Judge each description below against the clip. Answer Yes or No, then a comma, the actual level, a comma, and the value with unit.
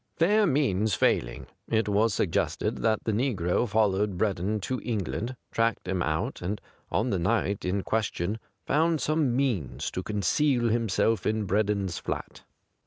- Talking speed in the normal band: Yes, average, 150 wpm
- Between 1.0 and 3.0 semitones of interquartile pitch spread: No, average, 3.7 semitones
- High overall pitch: No, low, 110 Hz